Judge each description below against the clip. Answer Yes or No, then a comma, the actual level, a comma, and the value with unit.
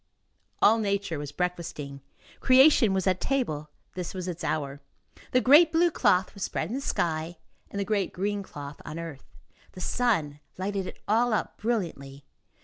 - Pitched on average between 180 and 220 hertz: Yes, medium, 185 Hz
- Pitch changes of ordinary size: No, wide, 5.7 semitones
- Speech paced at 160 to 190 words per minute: Yes, average, 165 wpm